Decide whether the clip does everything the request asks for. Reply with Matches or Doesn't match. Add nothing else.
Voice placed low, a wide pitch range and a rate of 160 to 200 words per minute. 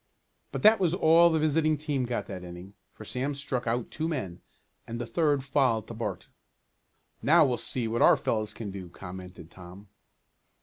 Matches